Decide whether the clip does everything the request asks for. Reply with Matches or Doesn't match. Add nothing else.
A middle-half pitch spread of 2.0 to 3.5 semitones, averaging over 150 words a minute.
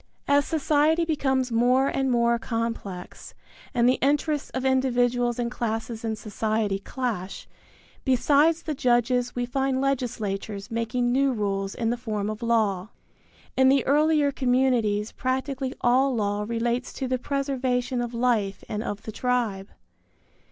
Doesn't match